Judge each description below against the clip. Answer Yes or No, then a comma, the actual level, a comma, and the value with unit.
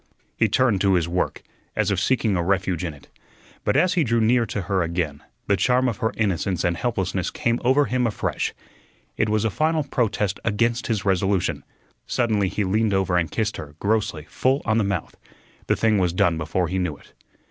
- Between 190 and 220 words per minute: Yes, average, 200 wpm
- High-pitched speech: No, low, 100 Hz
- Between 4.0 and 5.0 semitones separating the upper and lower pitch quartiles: Yes, average, 4.3 semitones